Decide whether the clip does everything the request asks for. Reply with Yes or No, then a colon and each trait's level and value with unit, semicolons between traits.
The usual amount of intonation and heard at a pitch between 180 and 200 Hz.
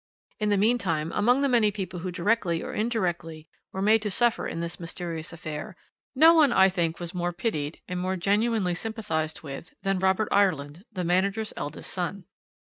Yes: average, 4.1 semitones; medium, 185 Hz